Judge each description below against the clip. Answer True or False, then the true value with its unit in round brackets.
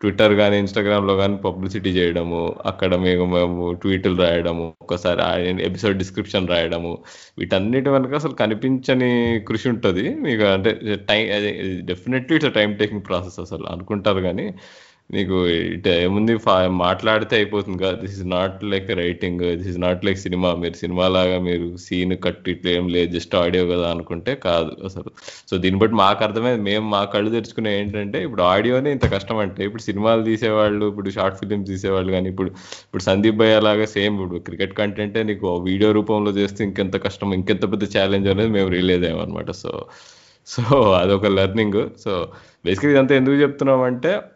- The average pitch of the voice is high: False (100 Hz)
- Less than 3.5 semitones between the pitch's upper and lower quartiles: True (2.9 semitones)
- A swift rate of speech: True (160 wpm)